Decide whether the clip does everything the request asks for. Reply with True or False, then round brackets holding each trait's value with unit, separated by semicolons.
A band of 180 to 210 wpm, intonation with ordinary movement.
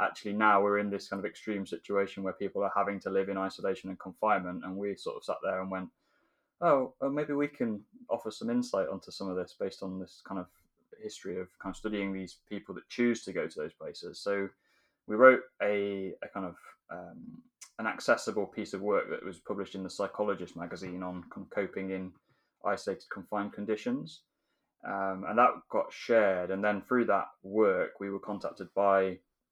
True (200 wpm; 3.6 semitones)